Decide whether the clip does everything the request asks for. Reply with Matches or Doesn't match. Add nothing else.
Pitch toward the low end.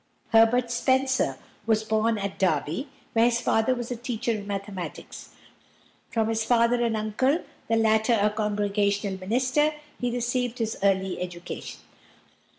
Doesn't match